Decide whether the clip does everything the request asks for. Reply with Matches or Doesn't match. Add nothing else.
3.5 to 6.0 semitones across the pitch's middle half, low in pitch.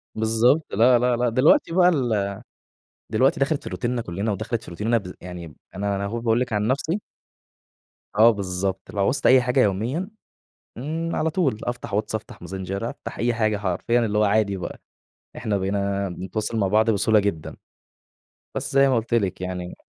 Matches